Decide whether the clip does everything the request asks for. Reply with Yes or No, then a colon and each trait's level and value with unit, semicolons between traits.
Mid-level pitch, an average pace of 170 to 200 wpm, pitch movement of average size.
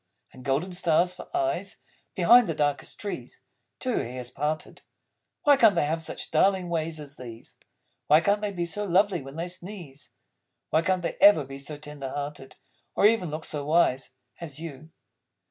Yes: medium, 160 Hz; average, 180 wpm; average, 4.5 semitones